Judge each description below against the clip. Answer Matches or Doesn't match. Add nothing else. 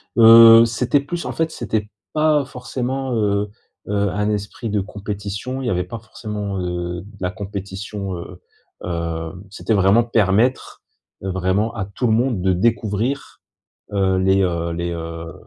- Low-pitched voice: Matches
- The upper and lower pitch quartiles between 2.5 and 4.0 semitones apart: Matches